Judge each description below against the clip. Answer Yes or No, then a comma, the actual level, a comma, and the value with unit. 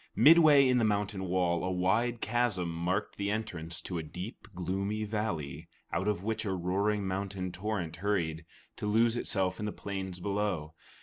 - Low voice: Yes, low, 100 Hz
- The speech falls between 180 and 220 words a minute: No, average, 170 wpm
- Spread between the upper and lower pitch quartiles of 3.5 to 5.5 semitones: No, average, 3.0 semitones